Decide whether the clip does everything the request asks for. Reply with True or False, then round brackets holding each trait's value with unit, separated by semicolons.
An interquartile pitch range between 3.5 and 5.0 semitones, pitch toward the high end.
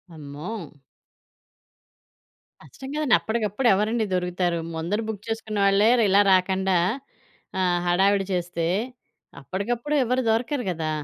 True (3.8 semitones; 195 Hz)